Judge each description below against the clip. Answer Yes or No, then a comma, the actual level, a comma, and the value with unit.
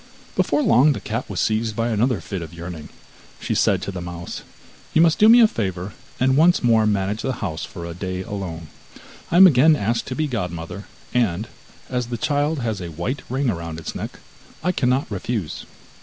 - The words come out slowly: No, average, 200 wpm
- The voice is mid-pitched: No, low, 110 Hz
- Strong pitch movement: Yes, wide, 6.5 semitones